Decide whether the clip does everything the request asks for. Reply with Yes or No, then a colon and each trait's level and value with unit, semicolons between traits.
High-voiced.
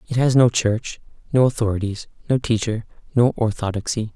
No: low, 115 Hz